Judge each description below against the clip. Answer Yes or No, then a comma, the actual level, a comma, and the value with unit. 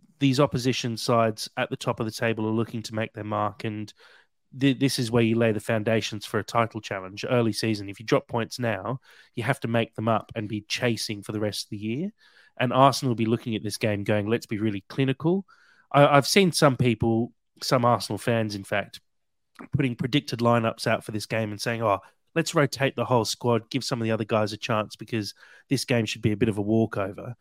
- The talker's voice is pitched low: Yes, low, 115 Hz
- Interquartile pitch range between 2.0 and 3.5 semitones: Yes, average, 2.9 semitones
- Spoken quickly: Yes, fast, 230 wpm